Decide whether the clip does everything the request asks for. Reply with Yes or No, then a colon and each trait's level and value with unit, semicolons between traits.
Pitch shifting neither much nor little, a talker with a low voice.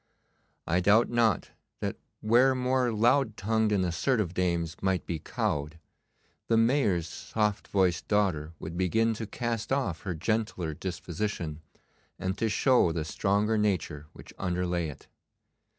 Yes: average, 4.7 semitones; low, 100 Hz